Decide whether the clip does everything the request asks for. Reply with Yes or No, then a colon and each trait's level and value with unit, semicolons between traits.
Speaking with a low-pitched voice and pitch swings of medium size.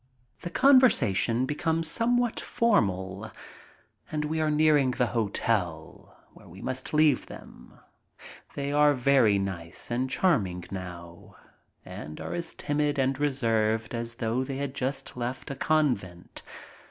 No: low, 130 Hz; wide, 6.3 semitones